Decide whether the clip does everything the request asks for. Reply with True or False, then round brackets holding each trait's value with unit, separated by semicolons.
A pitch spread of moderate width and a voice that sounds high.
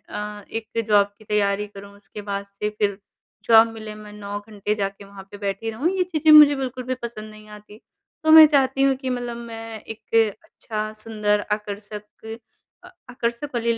False (2.3 semitones; 215 Hz)